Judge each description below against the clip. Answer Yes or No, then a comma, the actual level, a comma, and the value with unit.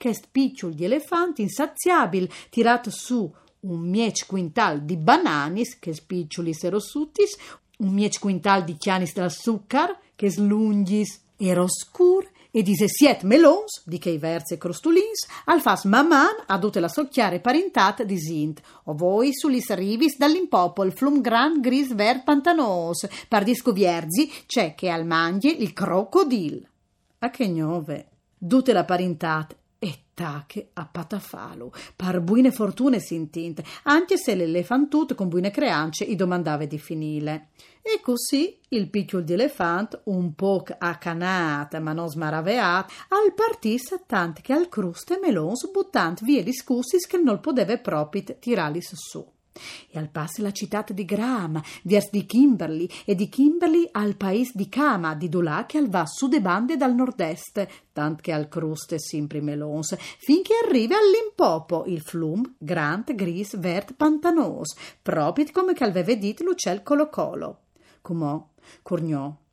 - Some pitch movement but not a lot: No, wide, 7.8 semitones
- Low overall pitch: No, high, 205 Hz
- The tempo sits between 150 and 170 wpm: No, average, 140 wpm